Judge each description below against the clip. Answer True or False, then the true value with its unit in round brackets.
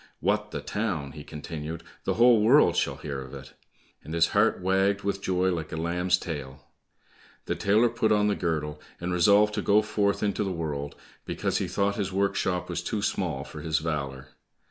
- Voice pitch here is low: True (90 Hz)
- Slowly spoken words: False (190 wpm)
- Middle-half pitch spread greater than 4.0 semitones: True (4.4 semitones)